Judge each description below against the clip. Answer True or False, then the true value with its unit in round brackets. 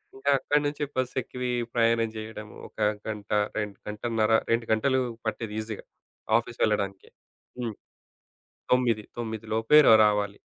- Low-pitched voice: True (110 Hz)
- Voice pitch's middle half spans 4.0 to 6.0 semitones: False (2.4 semitones)